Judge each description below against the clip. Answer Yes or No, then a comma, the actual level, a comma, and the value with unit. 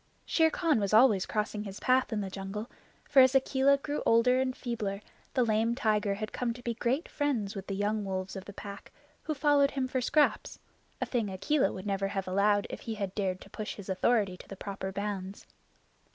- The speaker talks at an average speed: No, fast, 210 wpm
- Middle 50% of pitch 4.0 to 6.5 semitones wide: Yes, average, 4.5 semitones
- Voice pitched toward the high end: Yes, high, 215 Hz